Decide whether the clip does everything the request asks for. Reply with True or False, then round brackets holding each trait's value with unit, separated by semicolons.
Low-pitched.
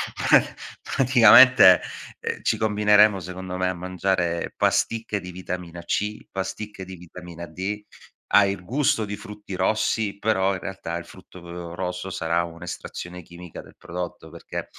True (95 Hz)